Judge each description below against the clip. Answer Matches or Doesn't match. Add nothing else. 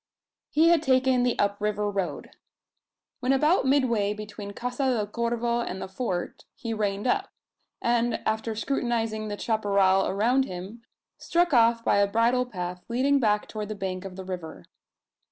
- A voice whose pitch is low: Doesn't match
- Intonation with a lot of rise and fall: Doesn't match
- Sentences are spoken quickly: Doesn't match